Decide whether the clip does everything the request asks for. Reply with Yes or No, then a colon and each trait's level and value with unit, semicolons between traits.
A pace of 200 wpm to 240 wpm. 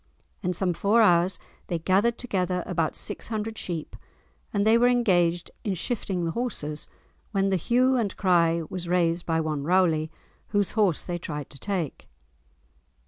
No: average, 160 wpm